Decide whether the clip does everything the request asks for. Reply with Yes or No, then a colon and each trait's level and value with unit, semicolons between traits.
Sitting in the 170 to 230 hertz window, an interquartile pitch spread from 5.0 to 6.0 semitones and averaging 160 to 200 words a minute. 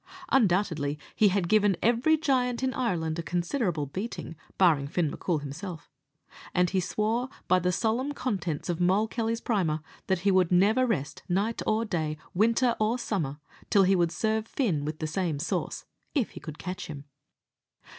Yes: high, 190 Hz; wide, 5.4 semitones; average, 170 wpm